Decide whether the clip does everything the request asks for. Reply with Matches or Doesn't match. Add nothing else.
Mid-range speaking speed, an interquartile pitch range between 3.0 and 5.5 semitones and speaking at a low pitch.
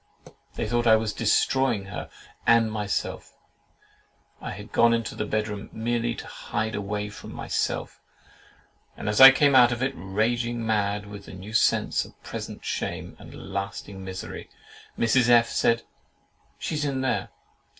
Doesn't match